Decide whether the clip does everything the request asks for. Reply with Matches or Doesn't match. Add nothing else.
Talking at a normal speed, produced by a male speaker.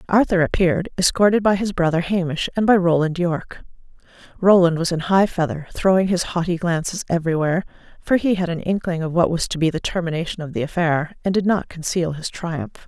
Doesn't match